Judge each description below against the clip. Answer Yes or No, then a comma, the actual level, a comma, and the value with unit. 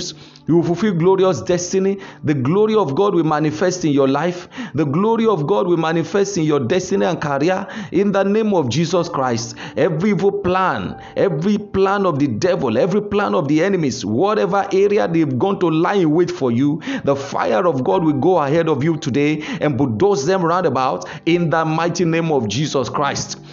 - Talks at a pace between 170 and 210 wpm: Yes, average, 195 wpm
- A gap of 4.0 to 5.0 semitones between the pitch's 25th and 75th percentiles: Yes, average, 4.3 semitones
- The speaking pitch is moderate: Yes, medium, 175 Hz